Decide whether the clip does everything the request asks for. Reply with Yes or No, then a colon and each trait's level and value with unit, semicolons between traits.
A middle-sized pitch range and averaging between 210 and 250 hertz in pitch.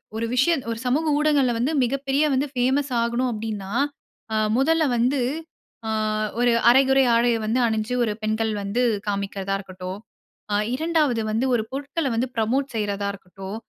Yes: average, 4.1 semitones; high, 240 Hz